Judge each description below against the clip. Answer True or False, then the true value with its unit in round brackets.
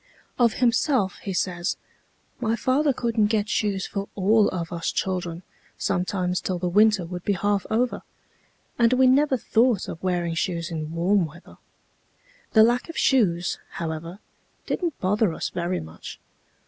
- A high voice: True (195 Hz)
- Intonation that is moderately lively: True (4.6 semitones)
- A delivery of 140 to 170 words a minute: True (150 wpm)